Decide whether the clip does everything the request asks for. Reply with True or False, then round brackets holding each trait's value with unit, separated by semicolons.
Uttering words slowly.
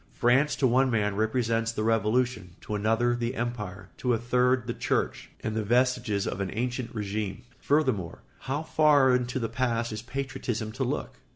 False (175 wpm)